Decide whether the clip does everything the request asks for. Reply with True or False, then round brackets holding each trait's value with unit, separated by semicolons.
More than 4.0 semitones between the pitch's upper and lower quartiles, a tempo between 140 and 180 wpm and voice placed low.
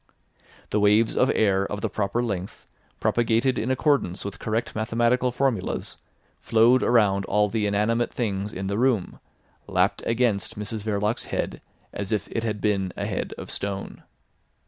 False (2.7 semitones; 155 wpm; 110 Hz)